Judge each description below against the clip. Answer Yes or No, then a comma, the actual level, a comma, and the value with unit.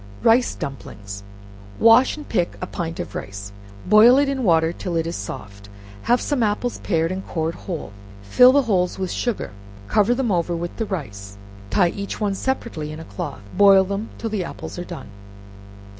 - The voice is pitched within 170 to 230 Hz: Yes, medium, 185 Hz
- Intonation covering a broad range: Yes, wide, 5.9 semitones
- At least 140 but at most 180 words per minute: No, average, 190 wpm